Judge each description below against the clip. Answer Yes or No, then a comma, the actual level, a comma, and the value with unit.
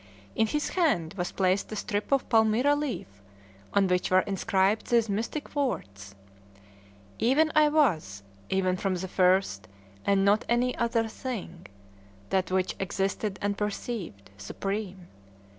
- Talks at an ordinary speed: No, slow, 130 wpm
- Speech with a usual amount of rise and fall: Yes, average, 4.2 semitones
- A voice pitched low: No, high, 200 Hz